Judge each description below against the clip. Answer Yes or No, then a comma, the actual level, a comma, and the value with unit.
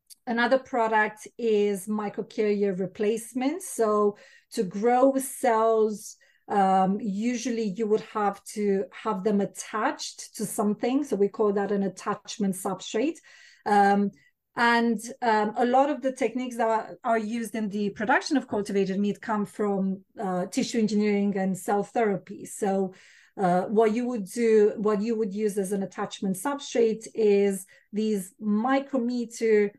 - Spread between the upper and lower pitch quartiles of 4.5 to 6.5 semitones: No, average, 2.7 semitones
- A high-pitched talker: Yes, high, 215 Hz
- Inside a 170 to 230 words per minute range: No, average, 140 wpm